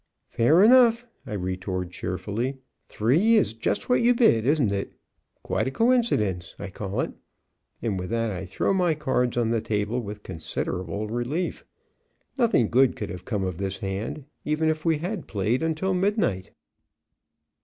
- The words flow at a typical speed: Yes, average, 160 wpm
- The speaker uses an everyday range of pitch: No, wide, 8.7 semitones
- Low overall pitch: Yes, low, 115 Hz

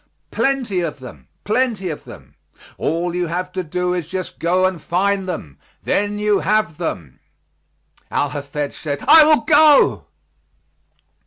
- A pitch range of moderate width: Yes, average, 4.3 semitones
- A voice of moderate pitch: Yes, medium, 180 Hz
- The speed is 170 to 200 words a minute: No, average, 145 wpm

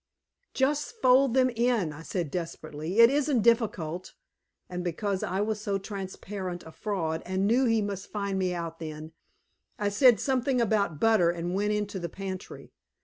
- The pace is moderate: Yes, average, 165 wpm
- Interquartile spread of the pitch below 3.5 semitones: No, average, 4.7 semitones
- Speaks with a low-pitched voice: No, high, 200 Hz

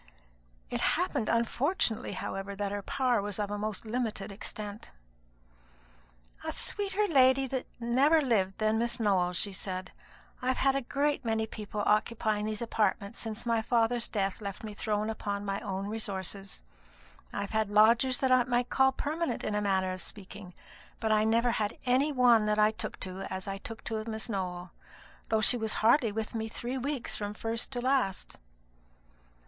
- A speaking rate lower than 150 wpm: No, average, 175 wpm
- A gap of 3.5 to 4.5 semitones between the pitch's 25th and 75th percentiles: No, average, 3.1 semitones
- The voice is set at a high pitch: Yes, high, 220 Hz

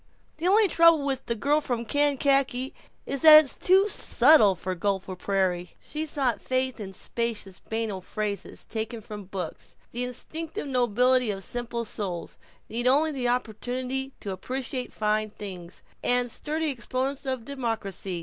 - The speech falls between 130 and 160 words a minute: Yes, average, 150 wpm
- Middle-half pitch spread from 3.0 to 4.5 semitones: No, average, 4.9 semitones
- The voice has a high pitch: Yes, high, 245 Hz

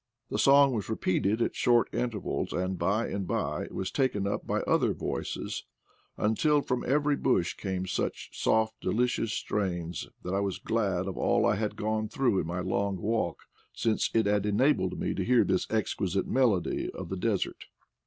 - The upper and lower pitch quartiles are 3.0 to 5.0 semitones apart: Yes, average, 3.5 semitones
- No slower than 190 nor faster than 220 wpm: No, average, 180 wpm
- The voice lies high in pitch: No, low, 105 Hz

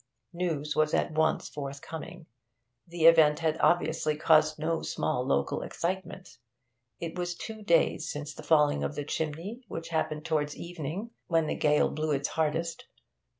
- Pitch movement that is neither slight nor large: No, narrow, 2.1 semitones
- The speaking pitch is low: No, medium, 160 Hz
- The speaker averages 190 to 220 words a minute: No, average, 150 wpm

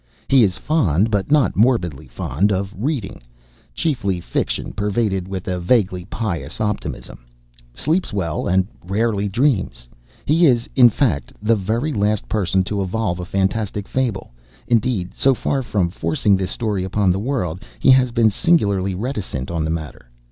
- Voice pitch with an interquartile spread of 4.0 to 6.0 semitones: Yes, average, 4.4 semitones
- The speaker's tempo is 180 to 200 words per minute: No, average, 155 wpm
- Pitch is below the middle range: Yes, low, 100 Hz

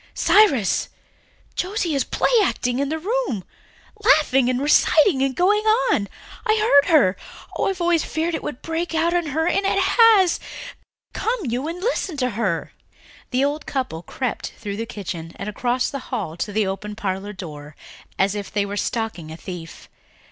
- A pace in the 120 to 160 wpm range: No, average, 175 wpm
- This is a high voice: Yes, very high, 270 Hz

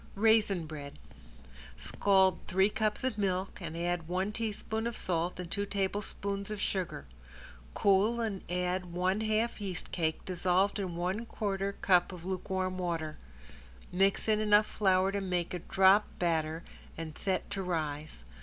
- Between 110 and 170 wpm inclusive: Yes, average, 150 wpm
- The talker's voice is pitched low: No, high, 190 Hz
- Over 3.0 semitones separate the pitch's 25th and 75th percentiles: No, narrow, 2.5 semitones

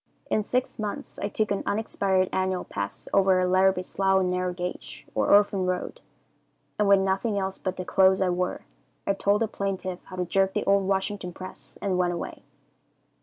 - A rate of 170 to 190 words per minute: Yes, average, 185 wpm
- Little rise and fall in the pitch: Yes, narrow, 1.5 semitones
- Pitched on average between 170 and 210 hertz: Yes, high, 190 Hz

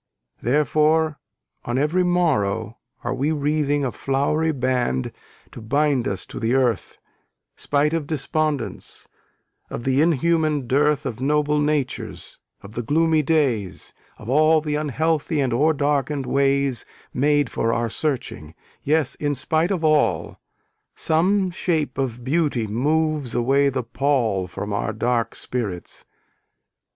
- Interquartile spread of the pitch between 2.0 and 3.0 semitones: No, average, 3.9 semitones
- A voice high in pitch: No, medium, 140 Hz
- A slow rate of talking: Yes, slow, 130 wpm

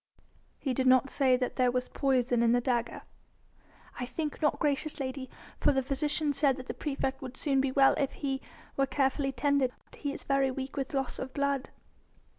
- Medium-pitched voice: No, very high, 270 Hz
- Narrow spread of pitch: Yes, narrow, 1.5 semitones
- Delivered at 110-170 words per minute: No, average, 195 wpm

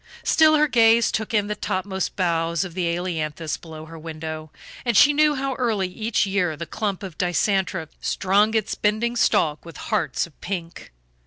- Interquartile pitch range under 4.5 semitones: No, average, 4.9 semitones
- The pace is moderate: Yes, average, 175 wpm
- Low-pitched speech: No, high, 190 Hz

